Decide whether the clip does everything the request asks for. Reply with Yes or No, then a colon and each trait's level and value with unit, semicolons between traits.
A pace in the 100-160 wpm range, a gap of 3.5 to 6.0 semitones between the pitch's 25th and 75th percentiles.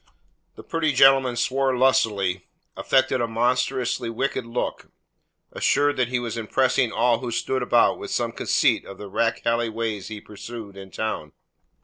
No: average, 150 wpm; average, 2.9 semitones